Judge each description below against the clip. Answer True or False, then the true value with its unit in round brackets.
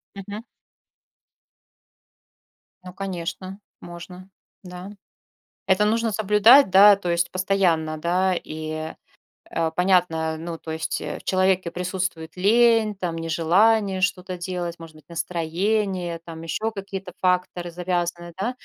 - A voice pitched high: False (180 Hz)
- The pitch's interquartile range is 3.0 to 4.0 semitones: False (2.6 semitones)